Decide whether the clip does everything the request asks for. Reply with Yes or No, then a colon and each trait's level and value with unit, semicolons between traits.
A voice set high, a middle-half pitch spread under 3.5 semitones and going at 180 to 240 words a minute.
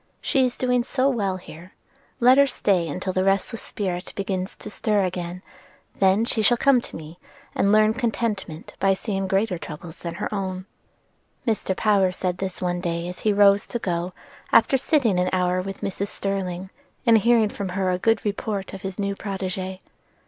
Yes: high, 195 Hz; average, 2.8 semitones; average, 185 wpm